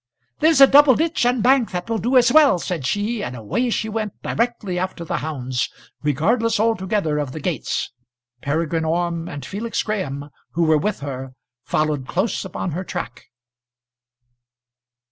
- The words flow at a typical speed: Yes, average, 160 wpm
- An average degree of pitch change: No, wide, 7.4 semitones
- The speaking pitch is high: No, medium, 180 Hz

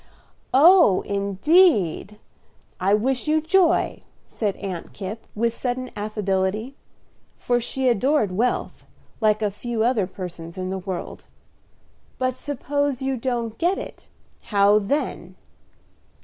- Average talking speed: No, slow, 120 wpm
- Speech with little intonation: No, average, 5.1 semitones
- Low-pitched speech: No, high, 225 Hz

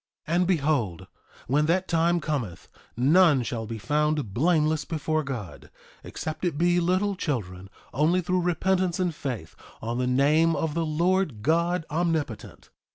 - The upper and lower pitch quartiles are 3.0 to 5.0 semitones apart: No, wide, 5.4 semitones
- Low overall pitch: No, medium, 155 Hz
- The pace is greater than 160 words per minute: No, average, 150 wpm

